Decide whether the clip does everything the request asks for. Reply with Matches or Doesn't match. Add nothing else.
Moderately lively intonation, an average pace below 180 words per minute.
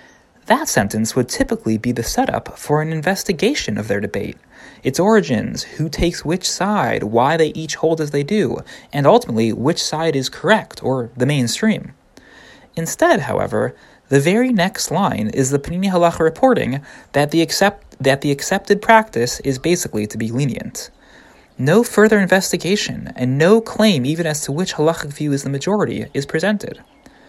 Doesn't match